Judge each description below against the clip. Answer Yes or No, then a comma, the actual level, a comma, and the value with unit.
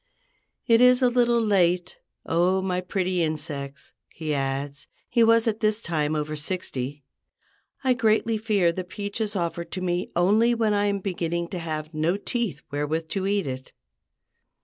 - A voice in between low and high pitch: Yes, medium, 180 Hz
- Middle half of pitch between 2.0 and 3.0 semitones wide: No, wide, 5.4 semitones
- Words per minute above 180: No, average, 160 wpm